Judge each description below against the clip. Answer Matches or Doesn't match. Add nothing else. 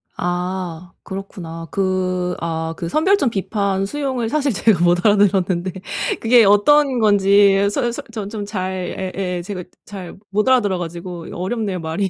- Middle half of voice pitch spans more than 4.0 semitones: Doesn't match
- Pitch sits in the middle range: Doesn't match